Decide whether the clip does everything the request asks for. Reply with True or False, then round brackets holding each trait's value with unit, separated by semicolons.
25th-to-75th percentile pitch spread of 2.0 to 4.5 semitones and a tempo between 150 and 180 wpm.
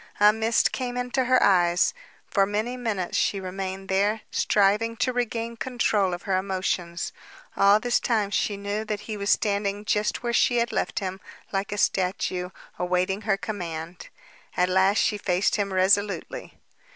True (2.7 semitones; 165 wpm)